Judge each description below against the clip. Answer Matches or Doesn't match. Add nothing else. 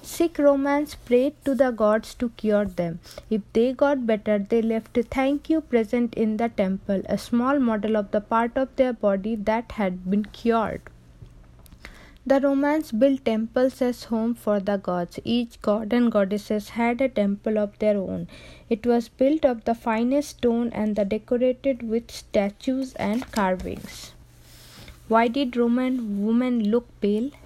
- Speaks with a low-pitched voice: Doesn't match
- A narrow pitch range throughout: Doesn't match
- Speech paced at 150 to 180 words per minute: Matches